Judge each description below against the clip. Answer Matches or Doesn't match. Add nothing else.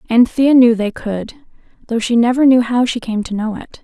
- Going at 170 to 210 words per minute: Doesn't match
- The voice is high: Matches